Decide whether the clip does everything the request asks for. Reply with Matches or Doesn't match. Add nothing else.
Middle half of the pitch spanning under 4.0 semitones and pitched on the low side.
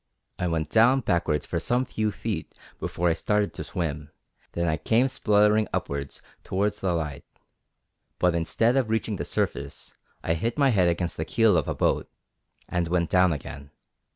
Doesn't match